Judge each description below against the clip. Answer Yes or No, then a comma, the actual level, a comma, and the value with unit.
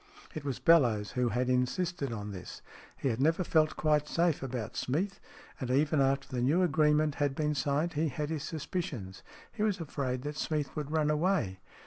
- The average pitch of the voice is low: No, medium, 150 Hz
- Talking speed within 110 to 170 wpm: No, average, 185 wpm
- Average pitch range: Yes, average, 3.8 semitones